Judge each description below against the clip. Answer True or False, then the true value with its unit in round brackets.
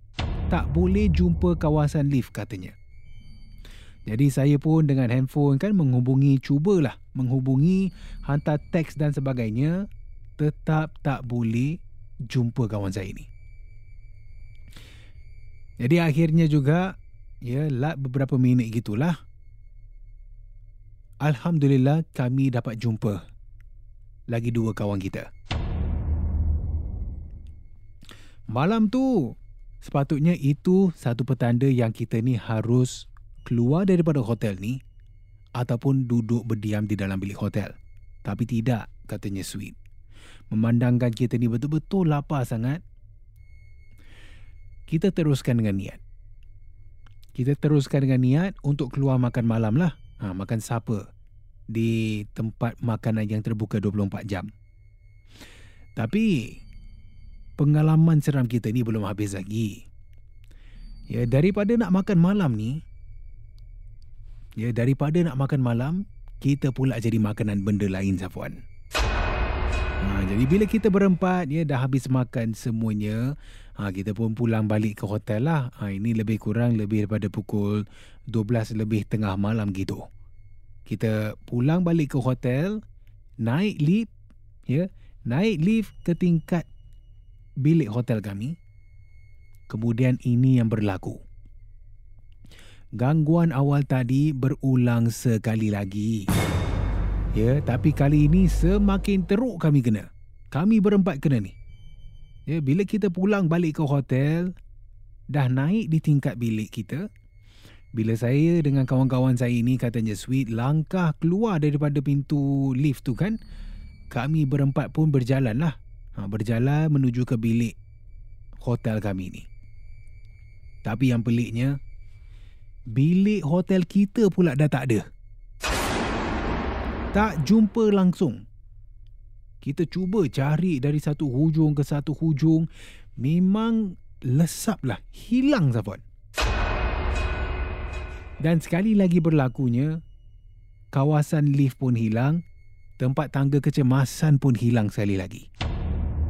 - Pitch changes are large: True (5.9 semitones)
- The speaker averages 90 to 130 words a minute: True (110 wpm)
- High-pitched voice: False (115 Hz)